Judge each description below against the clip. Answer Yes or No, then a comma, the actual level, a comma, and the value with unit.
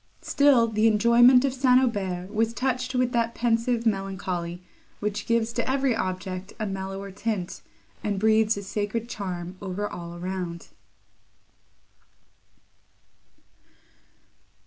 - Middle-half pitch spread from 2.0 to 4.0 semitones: Yes, average, 3.6 semitones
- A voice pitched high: Yes, high, 215 Hz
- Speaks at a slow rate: Yes, slow, 115 wpm